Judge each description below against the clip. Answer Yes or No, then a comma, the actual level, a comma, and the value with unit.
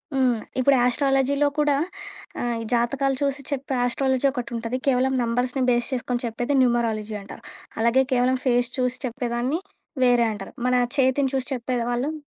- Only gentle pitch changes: Yes, narrow, 2.0 semitones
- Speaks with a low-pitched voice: No, very high, 250 Hz